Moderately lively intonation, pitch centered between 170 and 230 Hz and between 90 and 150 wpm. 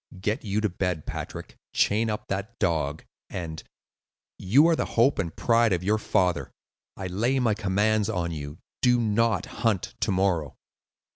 No: average, 4.1 semitones; low, 100 Hz; average, 145 wpm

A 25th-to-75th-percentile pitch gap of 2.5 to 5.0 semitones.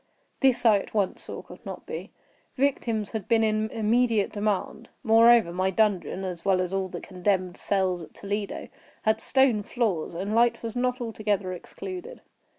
Yes: average, 3.4 semitones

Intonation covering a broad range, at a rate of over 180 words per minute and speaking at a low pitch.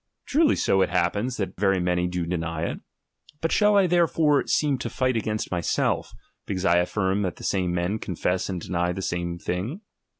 Yes: wide, 5.7 semitones; average, 190 wpm; very low, 95 Hz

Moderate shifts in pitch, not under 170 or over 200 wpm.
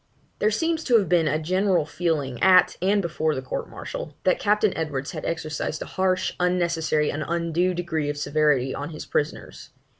Yes: average, 3.4 semitones; average, 180 wpm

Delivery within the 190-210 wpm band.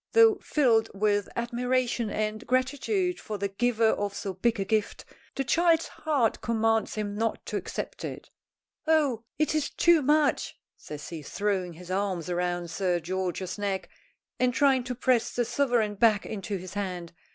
No: average, 165 wpm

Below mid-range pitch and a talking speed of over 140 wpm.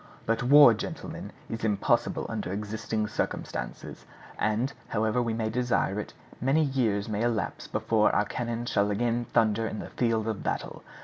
Yes: low, 110 Hz; average, 165 wpm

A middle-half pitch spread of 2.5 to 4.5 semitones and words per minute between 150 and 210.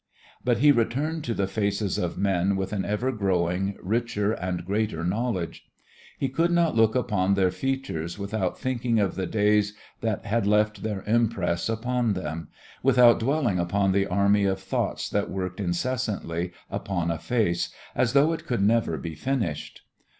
Yes: average, 4.0 semitones; average, 165 wpm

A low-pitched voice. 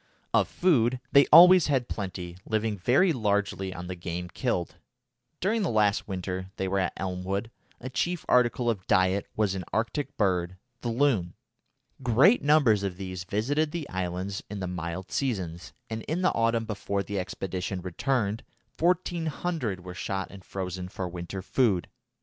Yes: low, 100 Hz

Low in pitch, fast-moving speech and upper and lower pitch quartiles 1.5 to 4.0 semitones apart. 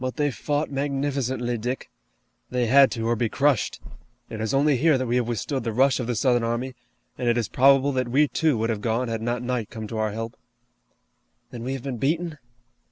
Yes: low, 125 Hz; fast, 220 wpm; average, 3.0 semitones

